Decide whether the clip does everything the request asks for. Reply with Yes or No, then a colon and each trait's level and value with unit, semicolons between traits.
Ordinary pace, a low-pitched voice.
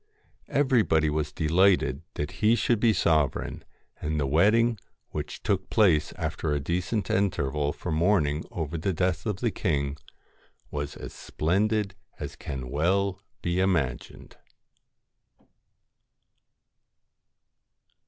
No: slow, 115 wpm; very low, 85 Hz